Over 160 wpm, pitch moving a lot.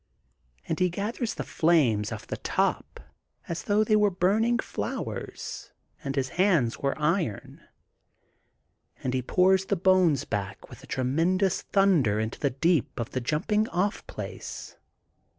No: average, 150 wpm; wide, 7.1 semitones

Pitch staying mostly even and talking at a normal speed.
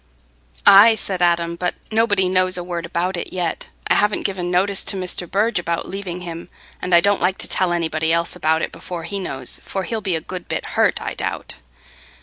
No: narrow, 2.2 semitones; fast, 210 wpm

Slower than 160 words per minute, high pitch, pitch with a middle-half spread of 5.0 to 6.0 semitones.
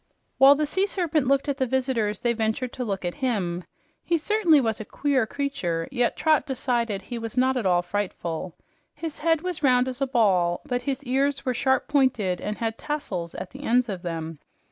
No: fast, 205 wpm; very high, 250 Hz; wide, 5.4 semitones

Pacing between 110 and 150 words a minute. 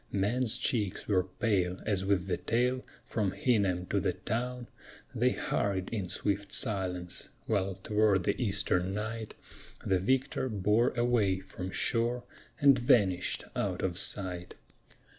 Yes: slow, 135 wpm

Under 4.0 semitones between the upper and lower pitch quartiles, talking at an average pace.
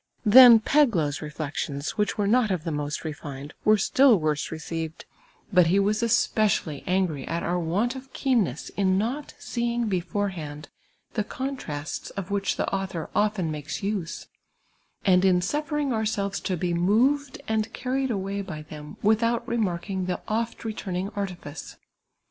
No: wide, 5.5 semitones; average, 150 wpm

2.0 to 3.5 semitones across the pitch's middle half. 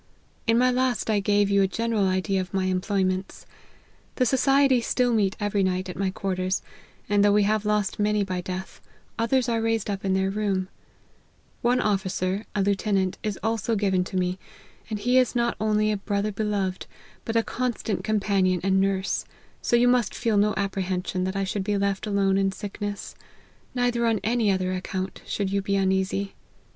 Yes: narrow, 2.4 semitones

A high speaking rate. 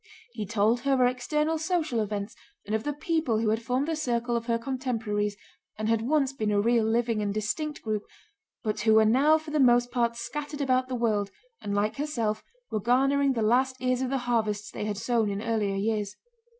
Yes: fast, 210 wpm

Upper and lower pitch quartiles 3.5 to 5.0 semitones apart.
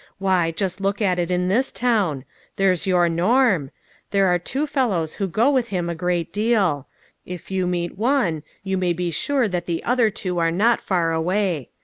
Yes: average, 3.8 semitones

